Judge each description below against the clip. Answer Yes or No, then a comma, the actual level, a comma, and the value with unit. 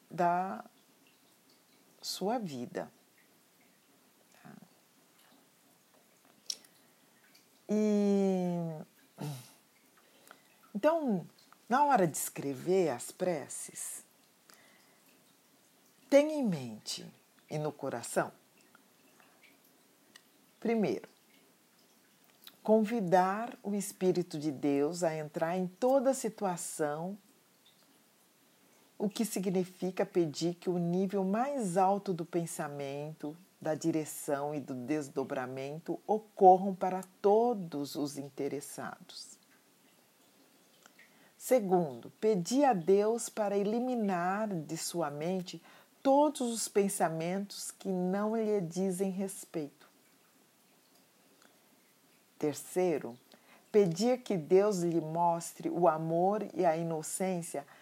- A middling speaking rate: No, slow, 80 wpm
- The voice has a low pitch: No, medium, 185 Hz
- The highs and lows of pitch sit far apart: No, average, 4.3 semitones